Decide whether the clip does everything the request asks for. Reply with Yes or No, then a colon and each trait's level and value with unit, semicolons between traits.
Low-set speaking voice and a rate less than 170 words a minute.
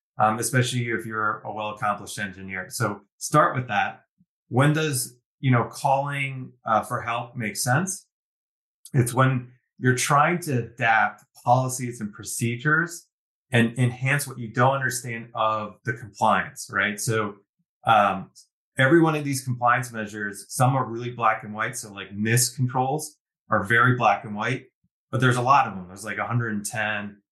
Yes: low, 120 Hz; average, 160 wpm